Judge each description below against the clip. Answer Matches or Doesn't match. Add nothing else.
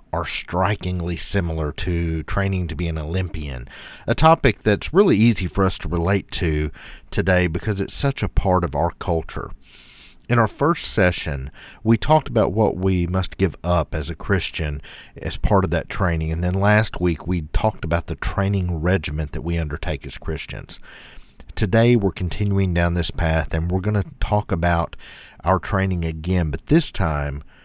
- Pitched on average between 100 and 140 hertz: Doesn't match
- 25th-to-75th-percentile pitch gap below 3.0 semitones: Doesn't match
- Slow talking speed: Doesn't match